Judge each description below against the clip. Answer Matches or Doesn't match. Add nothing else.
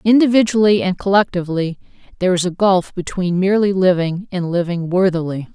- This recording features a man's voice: Doesn't match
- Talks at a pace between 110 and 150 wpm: Matches